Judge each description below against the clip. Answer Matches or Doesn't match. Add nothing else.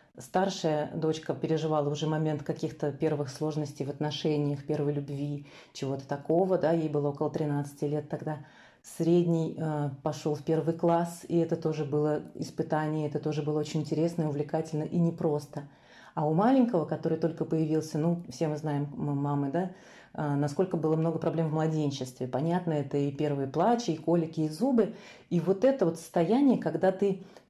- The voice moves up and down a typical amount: Doesn't match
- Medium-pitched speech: Matches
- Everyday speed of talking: Doesn't match